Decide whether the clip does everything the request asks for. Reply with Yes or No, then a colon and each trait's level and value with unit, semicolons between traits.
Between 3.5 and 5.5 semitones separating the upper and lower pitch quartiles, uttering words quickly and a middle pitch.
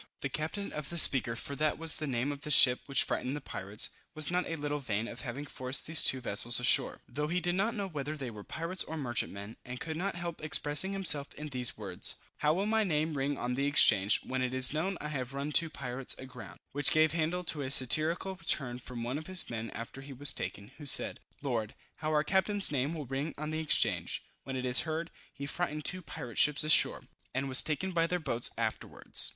Yes: average, 4.0 semitones; fast, 230 wpm; medium, 145 Hz